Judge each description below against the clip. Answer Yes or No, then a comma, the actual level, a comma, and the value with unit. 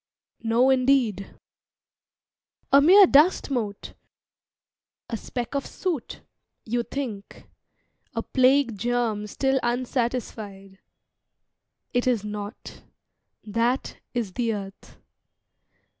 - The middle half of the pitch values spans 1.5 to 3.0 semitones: No, average, 4.0 semitones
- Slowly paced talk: Yes, slow, 90 wpm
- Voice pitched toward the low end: No, high, 240 Hz